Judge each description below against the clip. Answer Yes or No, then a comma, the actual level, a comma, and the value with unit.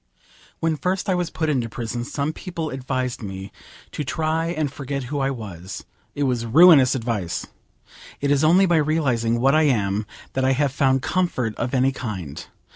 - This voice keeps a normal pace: Yes, average, 180 wpm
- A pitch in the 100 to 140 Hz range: Yes, low, 135 Hz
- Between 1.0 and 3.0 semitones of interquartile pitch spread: No, average, 4.9 semitones